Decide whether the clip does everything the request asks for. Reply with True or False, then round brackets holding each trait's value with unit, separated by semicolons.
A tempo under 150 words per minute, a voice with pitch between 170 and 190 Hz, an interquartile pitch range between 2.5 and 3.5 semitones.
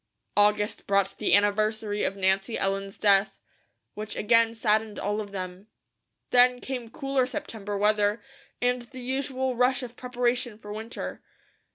False (140 wpm; 215 Hz; 3.2 semitones)